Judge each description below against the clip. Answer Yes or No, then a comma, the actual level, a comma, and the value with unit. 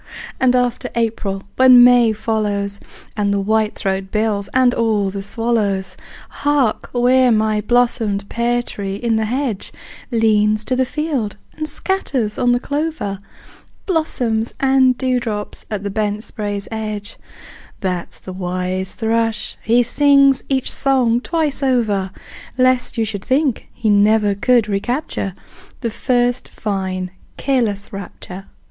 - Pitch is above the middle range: Yes, high, 225 Hz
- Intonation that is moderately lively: Yes, average, 3.7 semitones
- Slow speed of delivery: Yes, slow, 130 wpm